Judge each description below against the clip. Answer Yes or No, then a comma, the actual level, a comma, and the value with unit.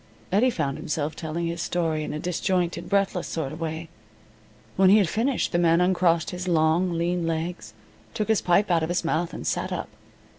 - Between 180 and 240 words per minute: Yes, average, 195 wpm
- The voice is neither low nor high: Yes, medium, 170 Hz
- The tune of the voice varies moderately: No, narrow, 2.2 semitones